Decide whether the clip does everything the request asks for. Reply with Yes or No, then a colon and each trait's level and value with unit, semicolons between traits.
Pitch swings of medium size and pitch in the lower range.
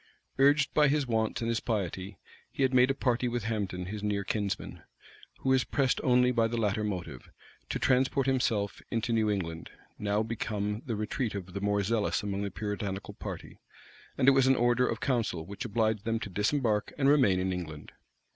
Yes: average, 3.7 semitones; low, 110 Hz